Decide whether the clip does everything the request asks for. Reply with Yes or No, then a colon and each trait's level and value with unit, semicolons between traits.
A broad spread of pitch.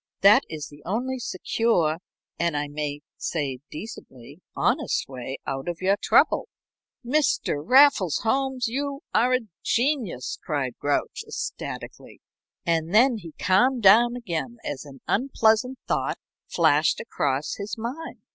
Yes: wide, 8.7 semitones